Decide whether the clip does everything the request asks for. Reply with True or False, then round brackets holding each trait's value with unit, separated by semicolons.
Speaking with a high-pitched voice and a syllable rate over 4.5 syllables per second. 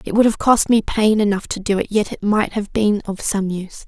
True (210 Hz; 5.4 syllables/s)